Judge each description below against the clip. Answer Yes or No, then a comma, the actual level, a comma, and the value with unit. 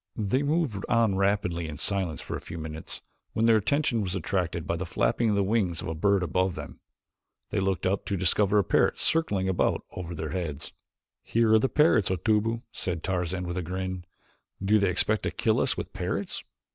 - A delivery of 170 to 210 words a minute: Yes, average, 200 wpm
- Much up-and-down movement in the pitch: No, average, 3.7 semitones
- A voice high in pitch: No, very low, 95 Hz